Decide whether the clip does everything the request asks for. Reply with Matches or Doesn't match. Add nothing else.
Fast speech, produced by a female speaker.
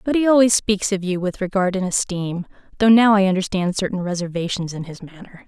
Matches